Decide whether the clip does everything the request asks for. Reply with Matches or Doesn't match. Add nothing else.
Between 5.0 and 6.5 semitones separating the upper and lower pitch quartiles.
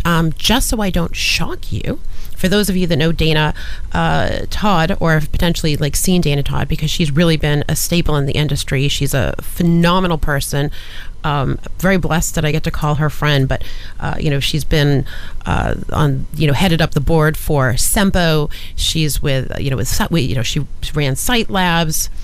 Doesn't match